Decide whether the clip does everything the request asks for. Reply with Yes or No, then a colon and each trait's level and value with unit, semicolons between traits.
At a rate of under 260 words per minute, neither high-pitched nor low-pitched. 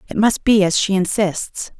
No: average, 200 wpm; high, 195 Hz